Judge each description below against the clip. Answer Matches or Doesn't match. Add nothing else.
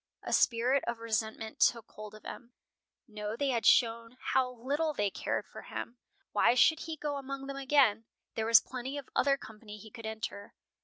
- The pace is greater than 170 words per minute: Matches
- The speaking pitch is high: Matches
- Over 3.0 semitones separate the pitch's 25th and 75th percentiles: Matches